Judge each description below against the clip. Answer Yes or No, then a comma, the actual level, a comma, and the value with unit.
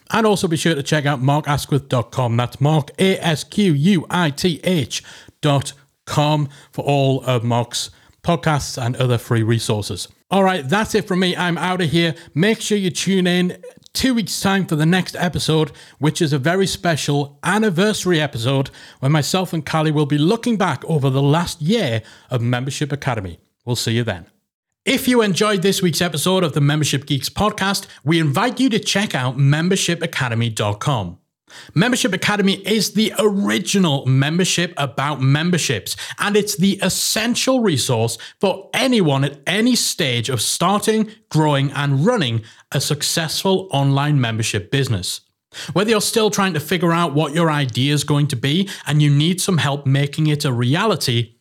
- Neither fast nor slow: Yes, average, 160 wpm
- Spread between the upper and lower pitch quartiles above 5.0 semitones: Yes, wide, 5.5 semitones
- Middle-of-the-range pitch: Yes, medium, 155 Hz